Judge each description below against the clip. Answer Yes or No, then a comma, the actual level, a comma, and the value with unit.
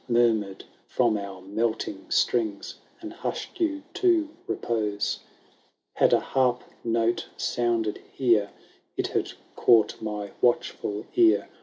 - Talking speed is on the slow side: Yes, slow, 115 wpm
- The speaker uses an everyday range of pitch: Yes, average, 3.2 semitones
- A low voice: Yes, low, 115 Hz